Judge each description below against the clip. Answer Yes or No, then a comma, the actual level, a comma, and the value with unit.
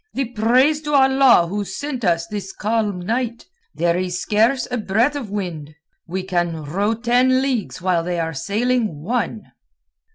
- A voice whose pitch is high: Yes, high, 210 Hz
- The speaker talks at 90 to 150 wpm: No, average, 160 wpm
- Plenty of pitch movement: Yes, wide, 5.8 semitones